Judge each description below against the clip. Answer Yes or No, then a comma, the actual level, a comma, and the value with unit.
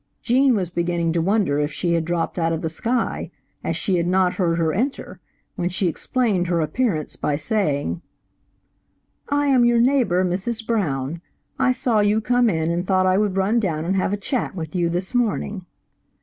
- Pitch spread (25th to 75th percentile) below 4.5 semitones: No, average, 5.3 semitones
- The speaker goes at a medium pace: Yes, average, 190 wpm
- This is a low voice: No, medium, 185 Hz